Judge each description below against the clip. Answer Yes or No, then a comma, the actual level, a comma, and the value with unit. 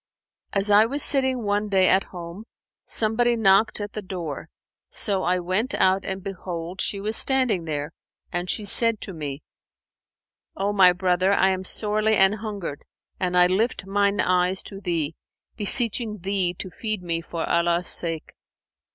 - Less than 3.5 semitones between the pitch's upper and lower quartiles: Yes, average, 3.0 semitones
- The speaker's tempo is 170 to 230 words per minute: No, average, 160 wpm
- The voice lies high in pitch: Yes, high, 195 Hz